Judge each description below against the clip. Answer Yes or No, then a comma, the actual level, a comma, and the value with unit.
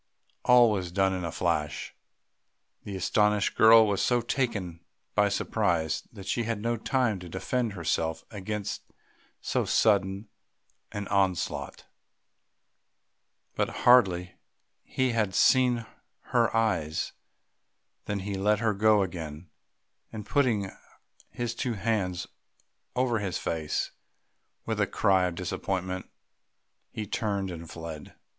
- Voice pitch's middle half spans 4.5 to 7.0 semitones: No, average, 3.7 semitones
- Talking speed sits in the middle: No, slow, 120 wpm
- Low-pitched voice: Yes, low, 100 Hz